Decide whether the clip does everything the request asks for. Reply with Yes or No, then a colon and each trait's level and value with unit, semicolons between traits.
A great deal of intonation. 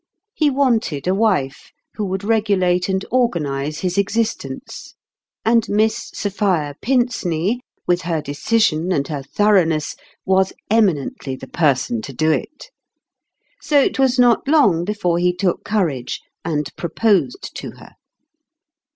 Yes: wide, 6.1 semitones